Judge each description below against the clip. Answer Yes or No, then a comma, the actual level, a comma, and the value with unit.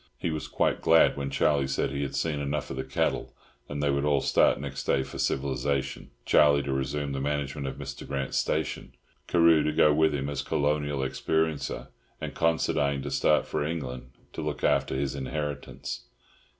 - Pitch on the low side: Yes, very low, 70 Hz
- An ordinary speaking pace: Yes, average, 180 wpm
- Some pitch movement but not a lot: No, narrow, 1.6 semitones